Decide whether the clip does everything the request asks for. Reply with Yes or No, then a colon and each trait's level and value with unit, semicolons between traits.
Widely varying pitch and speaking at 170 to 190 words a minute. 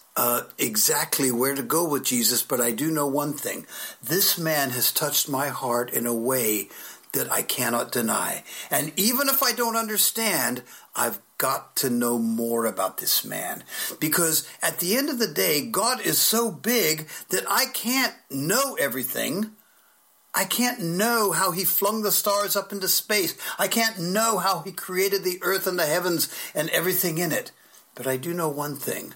Yes: wide, 6.9 semitones; average, 180 wpm